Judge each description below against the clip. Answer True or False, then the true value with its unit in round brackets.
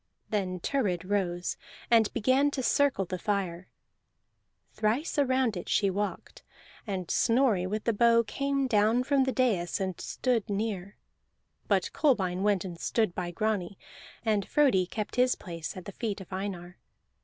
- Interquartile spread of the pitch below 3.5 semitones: False (4.8 semitones)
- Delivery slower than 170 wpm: True (155 wpm)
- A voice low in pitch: False (205 Hz)